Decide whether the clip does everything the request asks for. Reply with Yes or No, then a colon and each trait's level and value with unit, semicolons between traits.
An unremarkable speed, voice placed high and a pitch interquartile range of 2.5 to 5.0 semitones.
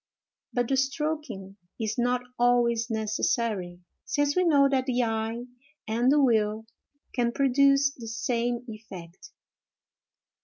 No: slow, 120 wpm; high, 240 Hz; average, 3.5 semitones